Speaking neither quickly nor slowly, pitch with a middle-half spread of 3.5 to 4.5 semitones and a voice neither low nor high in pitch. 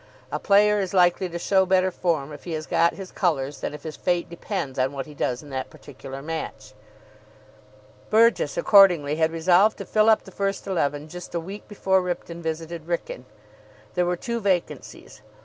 Yes: average, 185 wpm; average, 4.0 semitones; medium, 175 Hz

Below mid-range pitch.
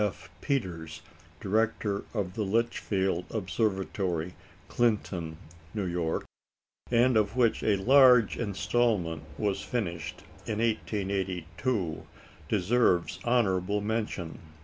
Yes: low, 100 Hz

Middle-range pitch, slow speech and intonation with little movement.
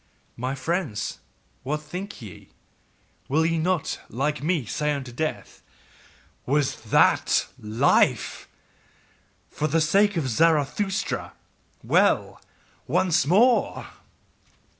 No: medium, 155 Hz; slow, 95 wpm; average, 4.6 semitones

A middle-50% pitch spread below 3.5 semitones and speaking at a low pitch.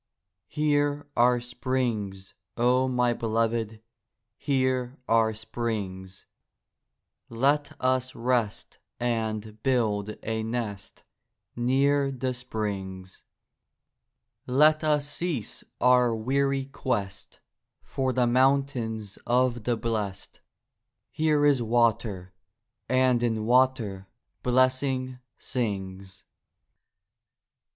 Yes: average, 3.0 semitones; low, 120 Hz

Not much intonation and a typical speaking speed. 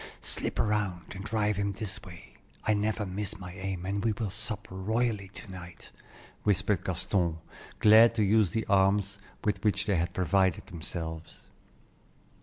Yes: narrow, 2.3 semitones; average, 155 wpm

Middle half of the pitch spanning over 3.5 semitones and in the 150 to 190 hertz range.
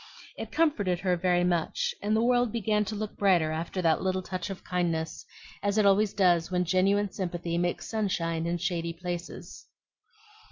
No: average, 2.8 semitones; medium, 185 Hz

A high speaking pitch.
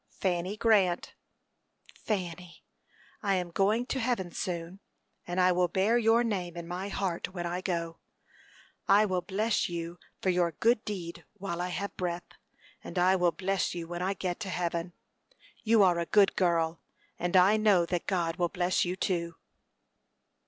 No: medium, 180 Hz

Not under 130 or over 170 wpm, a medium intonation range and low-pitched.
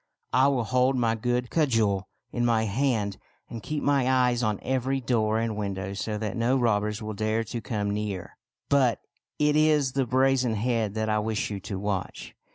No: average, 190 wpm; average, 3.3 semitones; low, 115 Hz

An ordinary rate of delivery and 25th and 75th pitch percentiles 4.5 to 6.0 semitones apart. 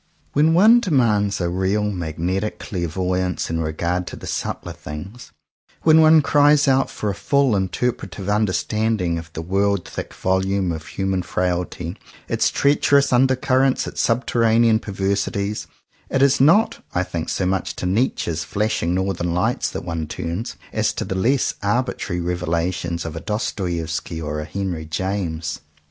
Yes: average, 150 wpm; average, 4.9 semitones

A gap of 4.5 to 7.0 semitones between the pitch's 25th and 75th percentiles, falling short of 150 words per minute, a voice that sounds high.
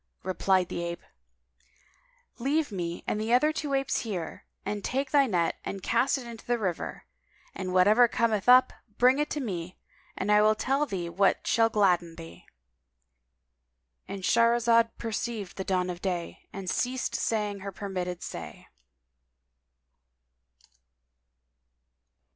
Yes: average, 5.2 semitones; slow, 135 wpm; high, 200 Hz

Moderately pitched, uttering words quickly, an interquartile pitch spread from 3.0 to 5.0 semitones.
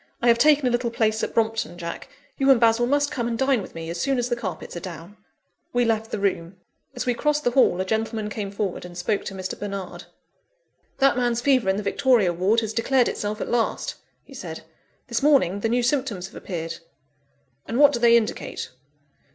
No: high, 225 Hz; fast, 215 wpm; average, 4.0 semitones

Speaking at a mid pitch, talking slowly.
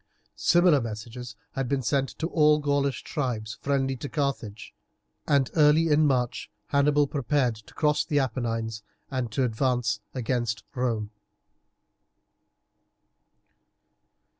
No: low, 130 Hz; slow, 115 wpm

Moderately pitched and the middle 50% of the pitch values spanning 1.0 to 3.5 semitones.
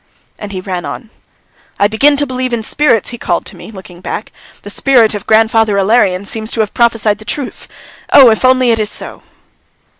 No: high, 220 Hz; average, 3.1 semitones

